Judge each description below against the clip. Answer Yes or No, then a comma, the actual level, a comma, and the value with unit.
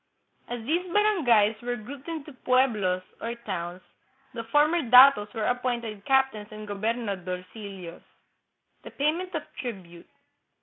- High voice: Yes, high, 235 Hz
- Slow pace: Yes, slow, 125 wpm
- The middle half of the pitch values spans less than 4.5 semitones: No, average, 4.9 semitones